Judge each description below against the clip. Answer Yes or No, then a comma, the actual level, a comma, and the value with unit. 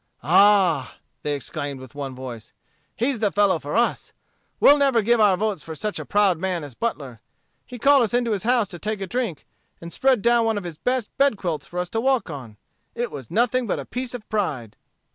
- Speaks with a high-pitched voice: Yes, high, 205 Hz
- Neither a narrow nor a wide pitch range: No, wide, 7.5 semitones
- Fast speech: Yes, fast, 220 wpm